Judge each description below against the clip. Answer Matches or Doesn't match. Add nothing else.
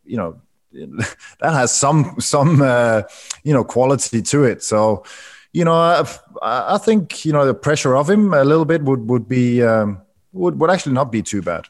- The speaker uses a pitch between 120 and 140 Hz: Matches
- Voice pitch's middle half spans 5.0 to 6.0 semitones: Matches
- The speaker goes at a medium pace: Matches